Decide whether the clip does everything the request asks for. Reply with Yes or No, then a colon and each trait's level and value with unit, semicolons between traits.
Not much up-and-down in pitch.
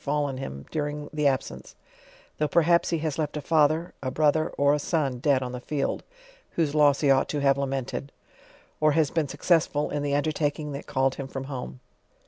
Yes: narrow, 1.9 semitones